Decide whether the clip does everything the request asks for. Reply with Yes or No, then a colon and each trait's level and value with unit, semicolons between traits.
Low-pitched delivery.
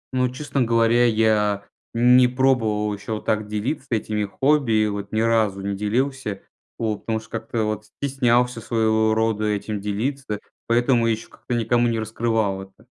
Yes: low, 110 Hz